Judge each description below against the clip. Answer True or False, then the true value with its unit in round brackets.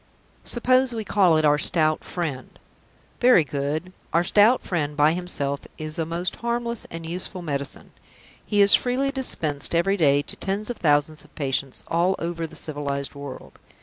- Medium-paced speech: True (165 wpm)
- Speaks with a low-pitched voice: False (165 Hz)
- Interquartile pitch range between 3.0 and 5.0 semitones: False (5.4 semitones)